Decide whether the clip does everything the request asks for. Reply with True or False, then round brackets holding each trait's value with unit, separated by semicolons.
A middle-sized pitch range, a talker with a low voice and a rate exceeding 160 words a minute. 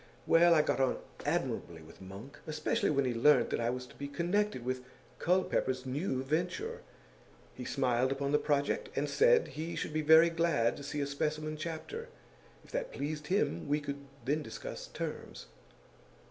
False (4.4 semitones; 150 Hz; 175 wpm)